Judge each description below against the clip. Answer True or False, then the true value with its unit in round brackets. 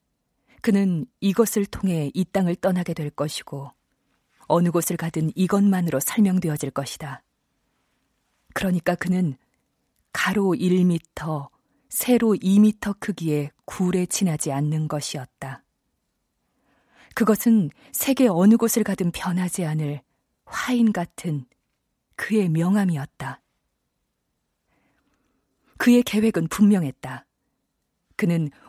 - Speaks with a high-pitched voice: False (180 Hz)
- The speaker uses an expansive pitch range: False (4.7 semitones)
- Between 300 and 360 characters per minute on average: False (215 characters per minute)